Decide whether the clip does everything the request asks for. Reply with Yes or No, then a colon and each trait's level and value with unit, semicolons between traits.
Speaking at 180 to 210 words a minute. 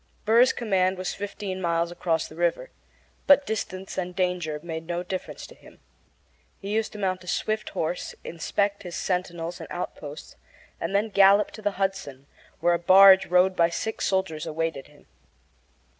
No: average, 165 wpm